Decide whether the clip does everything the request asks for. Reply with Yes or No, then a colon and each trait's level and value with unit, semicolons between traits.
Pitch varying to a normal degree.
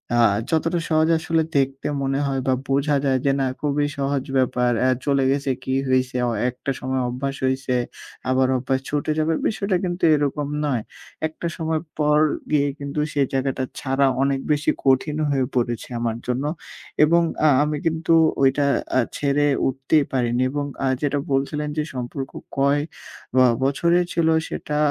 No: narrow, 2.2 semitones